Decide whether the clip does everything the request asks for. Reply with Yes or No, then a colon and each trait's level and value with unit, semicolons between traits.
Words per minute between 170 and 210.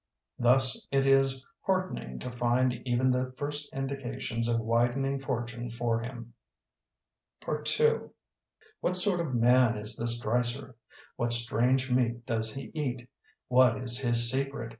No: slow, 135 wpm